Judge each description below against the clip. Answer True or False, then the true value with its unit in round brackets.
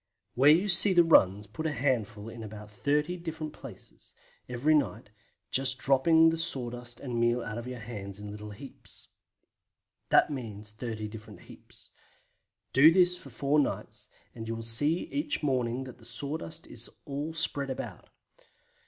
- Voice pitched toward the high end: False (125 Hz)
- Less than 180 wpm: True (165 wpm)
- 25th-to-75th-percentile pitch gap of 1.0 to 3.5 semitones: False (5.3 semitones)